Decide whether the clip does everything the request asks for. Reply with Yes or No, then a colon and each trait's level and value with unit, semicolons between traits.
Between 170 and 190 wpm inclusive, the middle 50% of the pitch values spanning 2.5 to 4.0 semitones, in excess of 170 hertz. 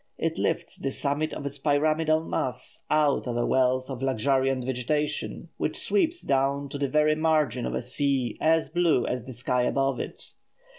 No: average, 180 wpm; average, 3.0 semitones; medium, 140 Hz